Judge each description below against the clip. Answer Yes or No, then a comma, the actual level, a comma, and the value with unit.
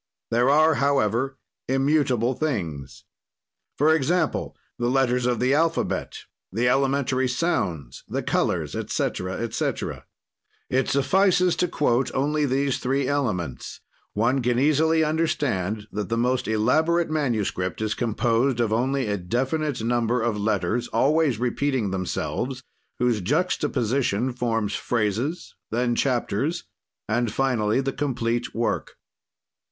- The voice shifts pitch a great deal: No, average, 4.0 semitones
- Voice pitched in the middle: No, low, 125 Hz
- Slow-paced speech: Yes, slow, 120 wpm